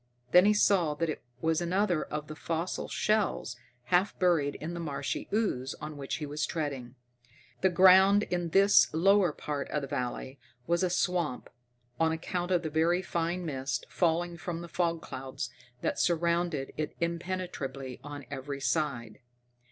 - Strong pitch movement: No, average, 3.8 semitones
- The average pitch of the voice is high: No, medium, 165 Hz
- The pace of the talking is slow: No, average, 160 wpm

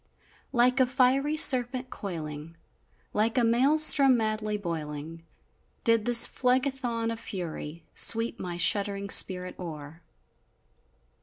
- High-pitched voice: Yes, high, 225 Hz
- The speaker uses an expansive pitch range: Yes, wide, 6.5 semitones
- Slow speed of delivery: Yes, slow, 105 wpm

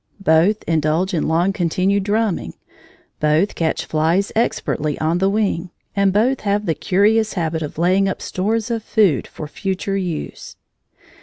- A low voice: No, high, 190 Hz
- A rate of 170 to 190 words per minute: No, average, 150 wpm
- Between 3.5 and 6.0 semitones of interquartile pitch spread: Yes, average, 4.1 semitones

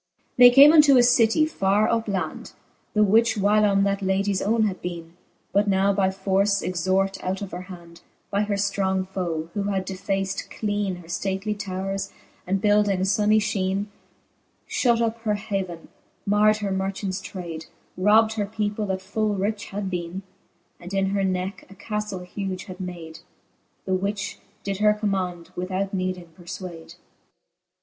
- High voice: Yes, high, 195 Hz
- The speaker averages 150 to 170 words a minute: Yes, average, 160 wpm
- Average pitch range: No, narrow, 2.0 semitones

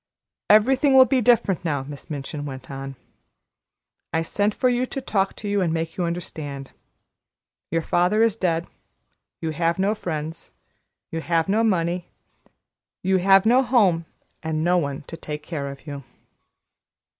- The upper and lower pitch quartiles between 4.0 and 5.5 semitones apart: Yes, average, 5.0 semitones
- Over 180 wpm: No, average, 160 wpm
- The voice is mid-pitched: Yes, medium, 170 Hz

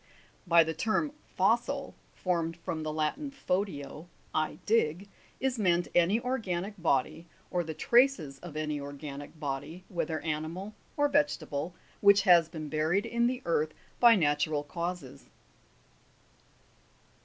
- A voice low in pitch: No, medium, 170 Hz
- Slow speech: Yes, slow, 130 wpm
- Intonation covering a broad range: No, average, 5.0 semitones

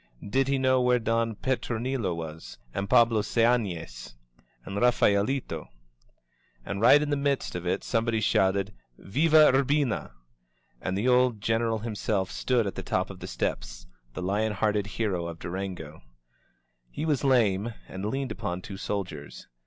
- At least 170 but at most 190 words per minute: No, average, 155 wpm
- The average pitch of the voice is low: Yes, low, 110 Hz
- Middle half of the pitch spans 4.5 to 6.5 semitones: Yes, average, 4.8 semitones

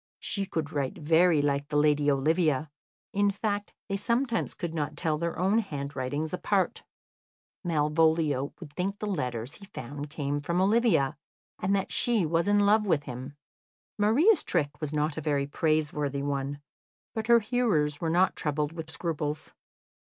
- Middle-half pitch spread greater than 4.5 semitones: Yes, average, 5.2 semitones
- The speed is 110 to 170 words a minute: Yes, average, 160 wpm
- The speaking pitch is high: No, medium, 160 Hz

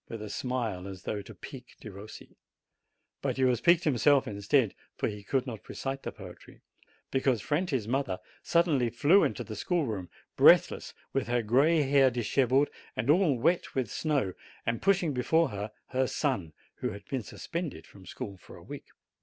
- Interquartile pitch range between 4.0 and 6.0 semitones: Yes, average, 5.2 semitones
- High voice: No, low, 125 Hz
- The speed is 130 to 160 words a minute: No, average, 175 wpm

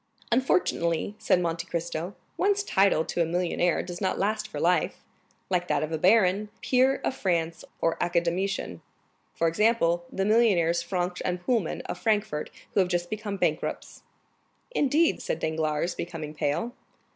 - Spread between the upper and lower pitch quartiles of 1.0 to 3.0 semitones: No, average, 4.0 semitones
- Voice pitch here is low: No, medium, 180 Hz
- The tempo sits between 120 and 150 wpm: Yes, average, 145 wpm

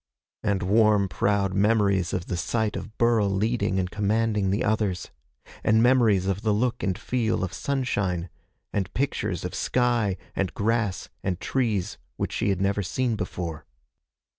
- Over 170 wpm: No, average, 155 wpm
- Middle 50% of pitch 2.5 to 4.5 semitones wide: Yes, average, 3.1 semitones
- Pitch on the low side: Yes, low, 100 Hz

